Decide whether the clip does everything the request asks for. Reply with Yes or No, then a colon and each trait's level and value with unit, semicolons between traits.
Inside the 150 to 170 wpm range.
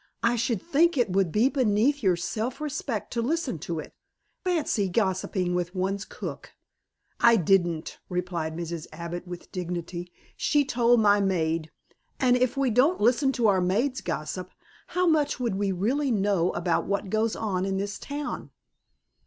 Yes: average, 160 wpm